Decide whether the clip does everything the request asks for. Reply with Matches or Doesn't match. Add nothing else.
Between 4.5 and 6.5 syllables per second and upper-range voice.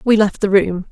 Matches